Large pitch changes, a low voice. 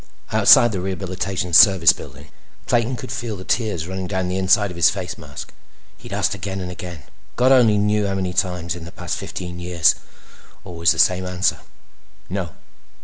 No: narrow, 2.5 semitones; very low, 95 Hz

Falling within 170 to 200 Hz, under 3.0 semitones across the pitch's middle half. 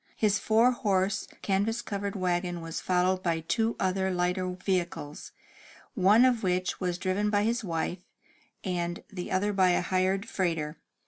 Yes: medium, 185 Hz; narrow, 2.4 semitones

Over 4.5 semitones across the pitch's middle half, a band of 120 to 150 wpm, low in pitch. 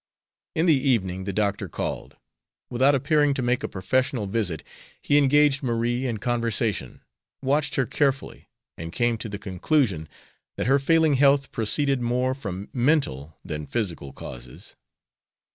Yes: wide, 5.5 semitones; average, 145 wpm; low, 120 Hz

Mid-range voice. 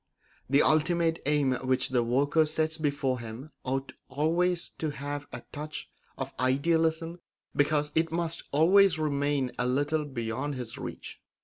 Yes: medium, 145 Hz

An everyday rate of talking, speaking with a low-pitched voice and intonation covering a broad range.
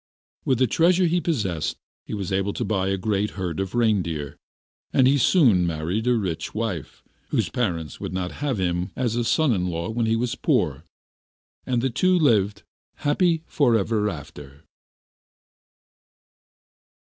Yes: average, 160 wpm; low, 105 Hz; wide, 5.7 semitones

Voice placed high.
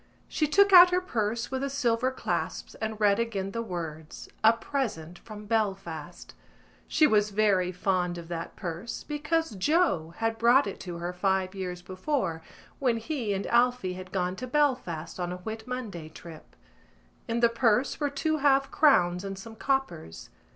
Yes: high, 215 Hz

